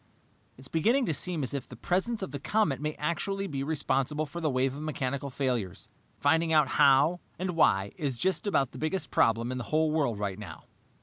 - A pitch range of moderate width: Yes, average, 4.2 semitones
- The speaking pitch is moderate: Yes, medium, 145 Hz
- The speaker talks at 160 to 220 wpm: Yes, fast, 205 wpm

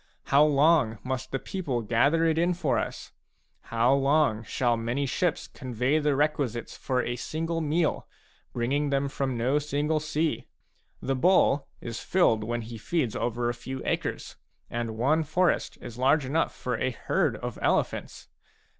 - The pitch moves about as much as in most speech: Yes, average, 4.4 semitones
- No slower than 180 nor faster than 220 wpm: No, average, 165 wpm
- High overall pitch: No, low, 135 Hz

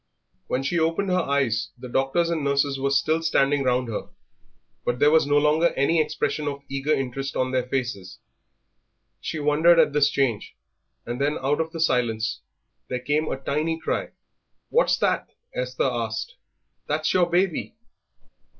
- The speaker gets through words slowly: No, average, 160 wpm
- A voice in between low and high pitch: Yes, medium, 145 Hz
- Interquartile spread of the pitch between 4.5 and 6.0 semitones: No, average, 3.5 semitones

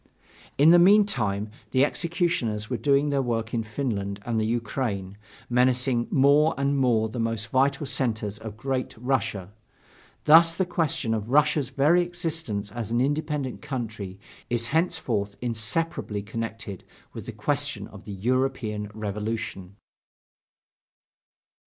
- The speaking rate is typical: No, slow, 130 wpm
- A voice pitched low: Yes, low, 120 Hz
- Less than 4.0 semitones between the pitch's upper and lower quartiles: No, average, 4.6 semitones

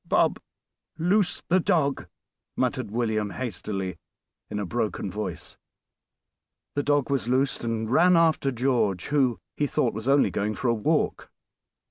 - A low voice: Yes, low, 125 Hz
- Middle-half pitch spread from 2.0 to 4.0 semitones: No, average, 5.1 semitones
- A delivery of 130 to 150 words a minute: Yes, average, 140 wpm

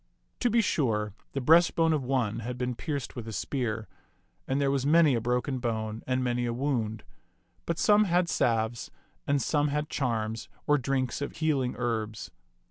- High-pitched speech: No, low, 130 Hz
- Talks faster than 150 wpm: Yes, average, 175 wpm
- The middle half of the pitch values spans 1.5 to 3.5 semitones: No, average, 4.2 semitones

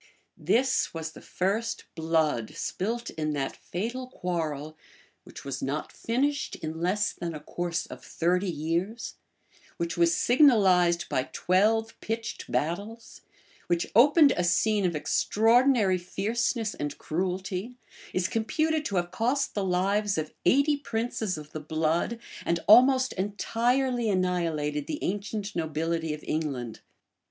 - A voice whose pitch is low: No, medium, 185 Hz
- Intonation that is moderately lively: No, wide, 5.8 semitones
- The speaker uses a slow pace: Yes, slow, 130 wpm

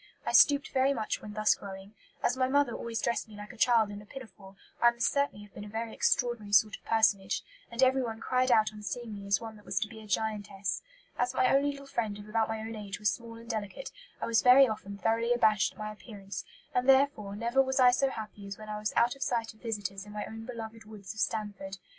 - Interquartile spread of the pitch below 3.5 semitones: Yes, average, 2.8 semitones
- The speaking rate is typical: No, fast, 250 wpm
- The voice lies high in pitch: Yes, high, 220 Hz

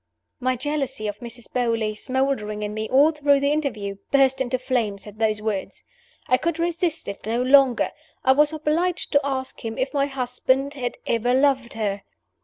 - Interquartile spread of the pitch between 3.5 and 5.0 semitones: Yes, average, 4.1 semitones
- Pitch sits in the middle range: No, very high, 260 Hz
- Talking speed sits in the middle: Yes, average, 180 wpm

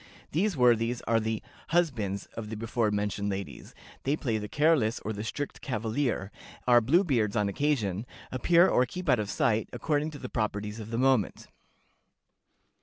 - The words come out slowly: No, average, 170 wpm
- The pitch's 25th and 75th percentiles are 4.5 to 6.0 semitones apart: Yes, average, 5.2 semitones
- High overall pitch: No, low, 115 Hz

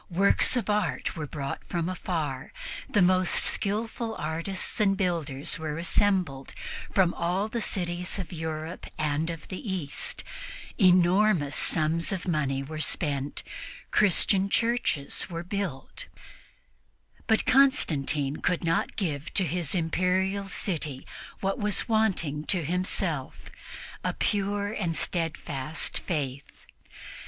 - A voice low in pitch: No, medium, 175 Hz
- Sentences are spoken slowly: Yes, slow, 120 wpm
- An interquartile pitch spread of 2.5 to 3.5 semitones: No, average, 4.2 semitones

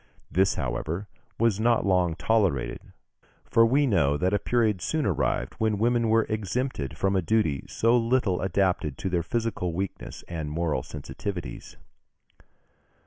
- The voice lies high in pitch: No, very low, 95 Hz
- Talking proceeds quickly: No, average, 140 wpm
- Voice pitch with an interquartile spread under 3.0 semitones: No, average, 5.1 semitones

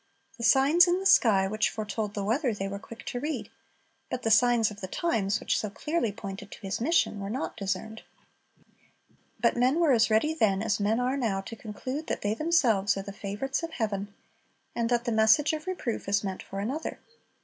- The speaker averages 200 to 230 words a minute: Yes, fast, 205 wpm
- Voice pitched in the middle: No, high, 225 Hz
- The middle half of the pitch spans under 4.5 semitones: No, average, 4.8 semitones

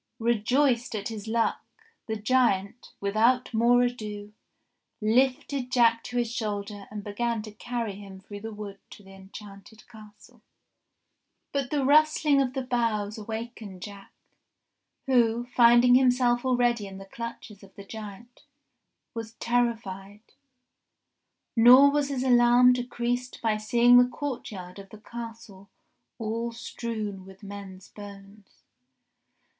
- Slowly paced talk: Yes, slow, 130 wpm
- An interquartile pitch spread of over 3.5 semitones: No, average, 3.2 semitones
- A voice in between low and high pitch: No, high, 230 Hz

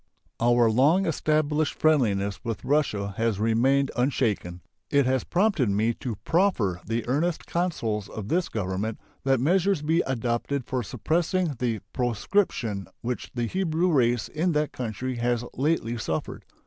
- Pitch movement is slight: No, wide, 5.6 semitones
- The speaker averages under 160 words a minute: Yes, average, 140 wpm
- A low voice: Yes, low, 125 Hz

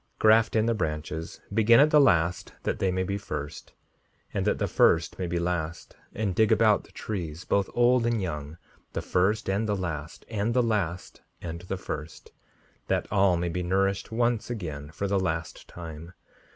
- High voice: No, very low, 95 Hz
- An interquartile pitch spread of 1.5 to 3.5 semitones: No, average, 4.8 semitones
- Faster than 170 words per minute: Yes, average, 190 wpm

